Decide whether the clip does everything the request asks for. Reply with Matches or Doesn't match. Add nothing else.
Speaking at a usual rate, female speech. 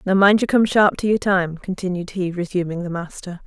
Doesn't match